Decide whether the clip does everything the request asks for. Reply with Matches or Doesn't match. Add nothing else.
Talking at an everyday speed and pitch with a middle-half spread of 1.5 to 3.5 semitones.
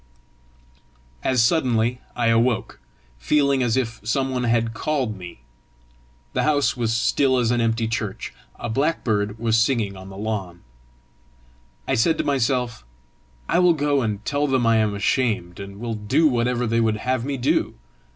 Matches